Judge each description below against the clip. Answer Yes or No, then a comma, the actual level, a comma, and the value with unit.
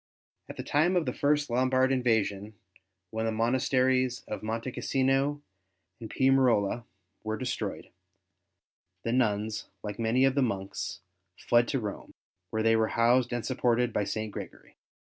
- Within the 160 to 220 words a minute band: No, average, 145 wpm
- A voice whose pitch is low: Yes, low, 120 Hz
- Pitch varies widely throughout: No, average, 3.0 semitones